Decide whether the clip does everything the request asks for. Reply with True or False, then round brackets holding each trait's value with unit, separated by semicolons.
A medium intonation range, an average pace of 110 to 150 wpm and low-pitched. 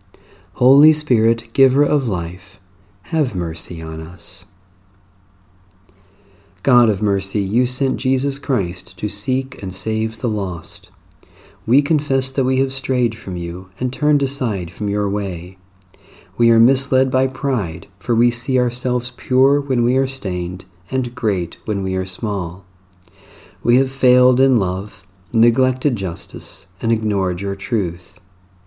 False (5.8 semitones; 140 wpm; 105 Hz)